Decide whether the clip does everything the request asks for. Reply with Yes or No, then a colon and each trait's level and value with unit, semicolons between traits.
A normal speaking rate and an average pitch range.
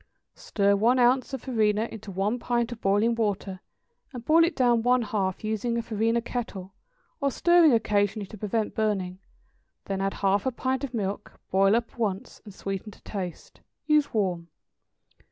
Yes: average, 170 wpm; average, 3.5 semitones